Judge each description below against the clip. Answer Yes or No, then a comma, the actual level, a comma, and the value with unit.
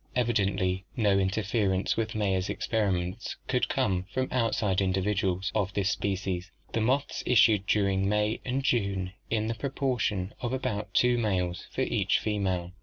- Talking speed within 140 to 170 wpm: Yes, average, 145 wpm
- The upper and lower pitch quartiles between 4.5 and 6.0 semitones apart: No, average, 3.3 semitones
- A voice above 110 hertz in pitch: No, low, 105 Hz